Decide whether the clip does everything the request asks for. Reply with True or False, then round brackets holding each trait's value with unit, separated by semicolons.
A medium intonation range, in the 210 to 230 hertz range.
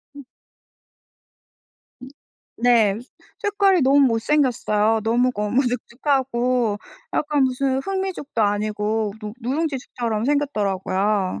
False (4.7 semitones; 245 Hz)